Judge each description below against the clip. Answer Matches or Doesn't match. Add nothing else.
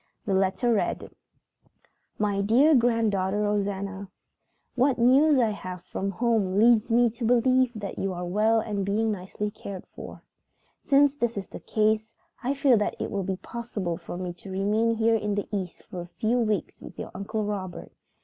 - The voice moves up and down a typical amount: Matches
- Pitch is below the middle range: Doesn't match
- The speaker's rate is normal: Matches